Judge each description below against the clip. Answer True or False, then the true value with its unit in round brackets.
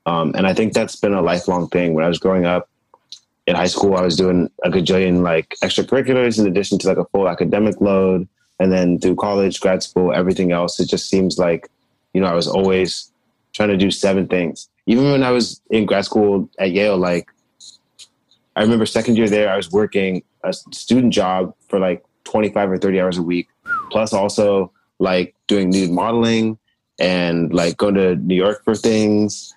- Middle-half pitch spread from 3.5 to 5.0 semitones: False (2.4 semitones)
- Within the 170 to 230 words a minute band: True (195 wpm)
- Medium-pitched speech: False (95 Hz)